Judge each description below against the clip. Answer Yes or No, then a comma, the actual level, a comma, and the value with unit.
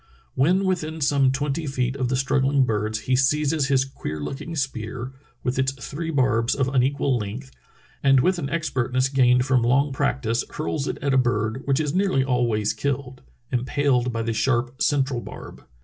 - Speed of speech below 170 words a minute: No, average, 180 wpm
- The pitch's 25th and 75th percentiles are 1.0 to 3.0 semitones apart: Yes, narrow, 2.4 semitones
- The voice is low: Yes, low, 130 Hz